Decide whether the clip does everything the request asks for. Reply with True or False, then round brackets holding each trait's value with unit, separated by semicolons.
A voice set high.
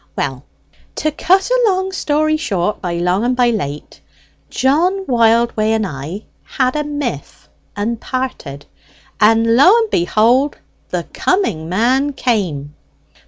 True (235 Hz)